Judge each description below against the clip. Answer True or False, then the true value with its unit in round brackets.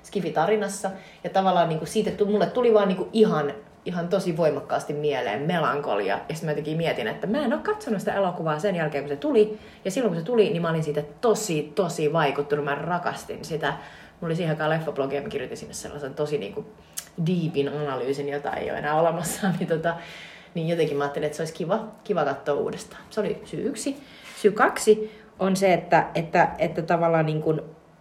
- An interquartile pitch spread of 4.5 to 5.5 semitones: True (5.2 semitones)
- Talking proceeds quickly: True (195 wpm)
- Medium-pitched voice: True (170 Hz)